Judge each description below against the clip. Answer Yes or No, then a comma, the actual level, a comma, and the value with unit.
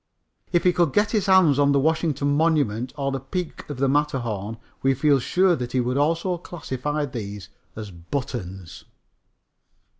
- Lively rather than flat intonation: No, average, 4.8 semitones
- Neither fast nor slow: Yes, average, 160 wpm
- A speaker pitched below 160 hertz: Yes, medium, 140 Hz